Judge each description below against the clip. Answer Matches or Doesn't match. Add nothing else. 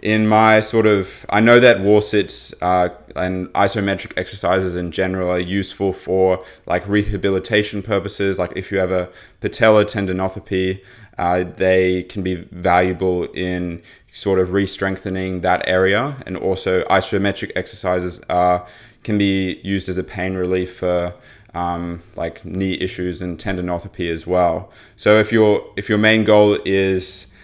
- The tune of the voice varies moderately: Doesn't match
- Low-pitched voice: Matches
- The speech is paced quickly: Doesn't match